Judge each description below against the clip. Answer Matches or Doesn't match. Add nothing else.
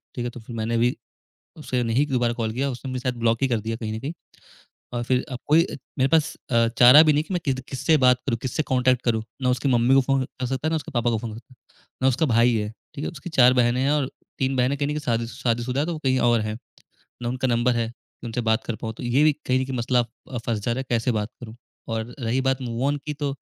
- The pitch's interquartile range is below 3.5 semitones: Matches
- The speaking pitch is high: Doesn't match